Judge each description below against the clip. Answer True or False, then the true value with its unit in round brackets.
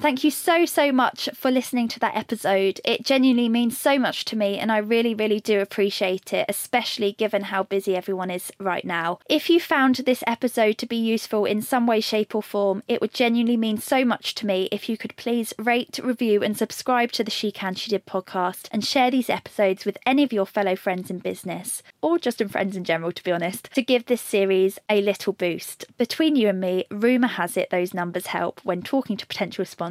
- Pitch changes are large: False (4.0 semitones)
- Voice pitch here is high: True (215 Hz)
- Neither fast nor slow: False (225 wpm)